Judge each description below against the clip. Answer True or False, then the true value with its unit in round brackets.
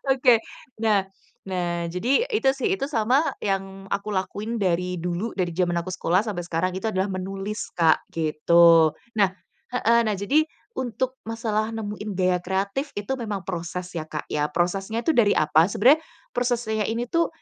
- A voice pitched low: False (200 Hz)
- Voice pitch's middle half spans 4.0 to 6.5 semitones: True (4.5 semitones)